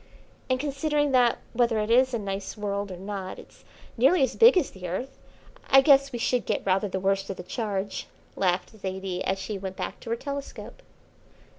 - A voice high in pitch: Yes, high, 215 Hz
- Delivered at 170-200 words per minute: Yes, average, 195 wpm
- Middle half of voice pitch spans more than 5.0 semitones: Yes, wide, 5.4 semitones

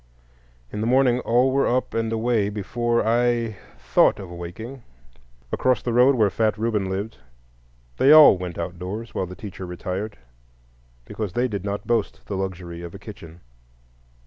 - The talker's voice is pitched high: No, low, 110 Hz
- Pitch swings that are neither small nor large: Yes, average, 4.1 semitones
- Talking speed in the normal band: Yes, average, 160 wpm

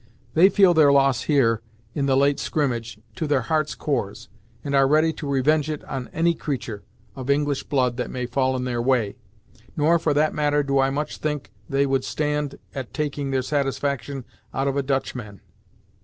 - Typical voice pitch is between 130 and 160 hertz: Yes, medium, 140 Hz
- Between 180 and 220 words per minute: Yes, average, 190 wpm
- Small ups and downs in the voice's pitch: Yes, narrow, 2.2 semitones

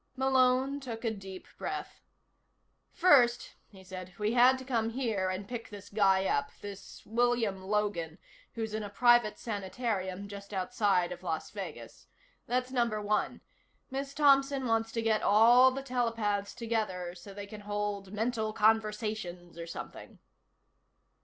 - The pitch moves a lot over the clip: No, average, 3.5 semitones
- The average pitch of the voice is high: Yes, high, 215 Hz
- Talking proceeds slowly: No, average, 145 wpm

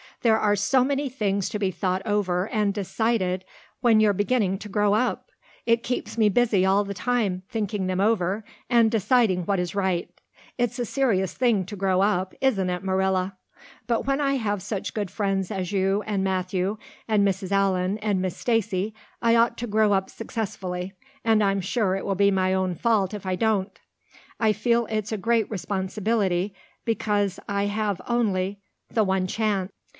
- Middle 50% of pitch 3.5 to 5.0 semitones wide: No, average, 2.7 semitones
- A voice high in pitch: Yes, high, 205 Hz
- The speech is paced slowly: No, average, 180 wpm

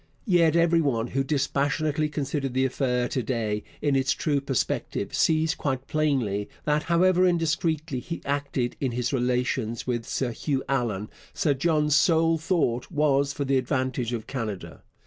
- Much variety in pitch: No, average, 3.8 semitones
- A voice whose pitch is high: No, medium, 140 Hz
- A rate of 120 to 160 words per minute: Yes, average, 155 wpm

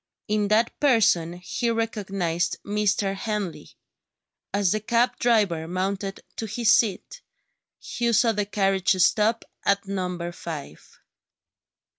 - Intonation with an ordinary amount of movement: Yes, average, 3.3 semitones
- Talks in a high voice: Yes, high, 200 Hz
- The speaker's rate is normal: No, slow, 115 wpm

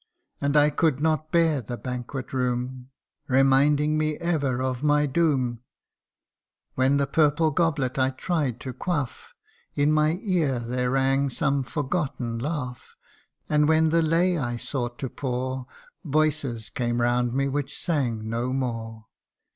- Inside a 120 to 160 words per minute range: Yes, average, 140 wpm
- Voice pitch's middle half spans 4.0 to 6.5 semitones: No, average, 3.6 semitones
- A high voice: No, low, 135 Hz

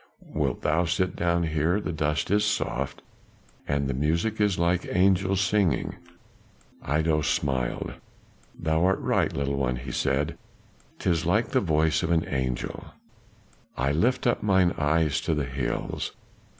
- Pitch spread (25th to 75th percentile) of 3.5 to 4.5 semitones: Yes, average, 4.1 semitones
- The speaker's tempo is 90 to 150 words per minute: Yes, average, 145 wpm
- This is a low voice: Yes, very low, 80 Hz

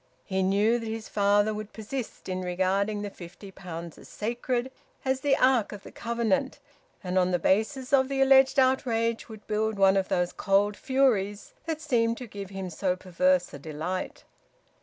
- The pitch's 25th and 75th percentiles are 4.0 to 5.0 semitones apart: Yes, average, 4.3 semitones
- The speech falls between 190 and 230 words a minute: No, average, 180 wpm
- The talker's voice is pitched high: Yes, high, 210 Hz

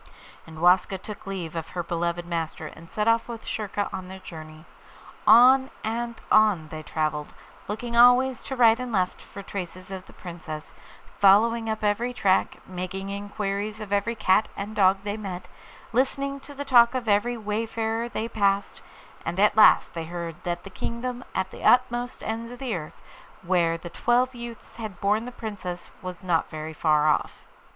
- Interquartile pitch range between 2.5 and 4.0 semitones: No, average, 4.7 semitones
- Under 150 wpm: No, average, 175 wpm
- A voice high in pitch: Yes, high, 205 Hz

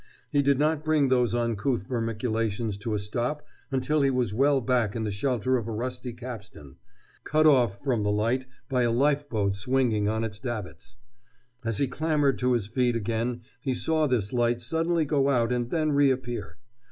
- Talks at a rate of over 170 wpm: Yes, average, 180 wpm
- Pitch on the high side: No, low, 125 Hz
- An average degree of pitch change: Yes, average, 3.5 semitones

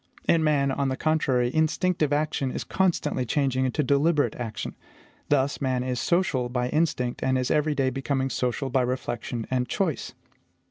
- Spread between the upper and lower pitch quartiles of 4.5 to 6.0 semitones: No, average, 3.2 semitones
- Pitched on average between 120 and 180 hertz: Yes, low, 135 Hz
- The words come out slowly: No, average, 165 wpm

